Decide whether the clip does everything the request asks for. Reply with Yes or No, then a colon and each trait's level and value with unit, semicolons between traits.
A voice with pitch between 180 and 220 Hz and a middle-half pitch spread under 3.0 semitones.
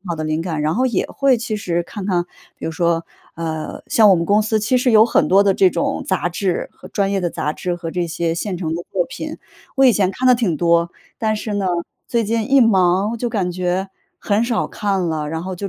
No: high, 190 Hz; average, 4.0 semitones